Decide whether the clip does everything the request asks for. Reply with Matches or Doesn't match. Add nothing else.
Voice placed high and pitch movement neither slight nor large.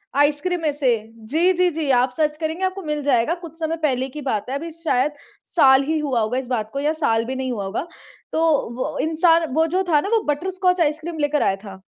Matches